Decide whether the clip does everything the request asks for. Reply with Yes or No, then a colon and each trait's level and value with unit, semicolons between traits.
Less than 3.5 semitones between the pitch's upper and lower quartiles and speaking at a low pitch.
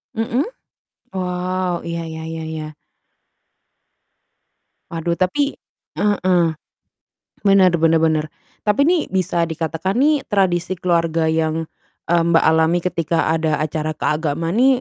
No: narrow, 2.6 semitones; medium, 170 Hz